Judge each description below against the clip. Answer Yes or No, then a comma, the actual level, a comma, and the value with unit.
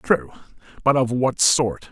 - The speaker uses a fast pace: No, average, 155 wpm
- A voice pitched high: No, low, 125 Hz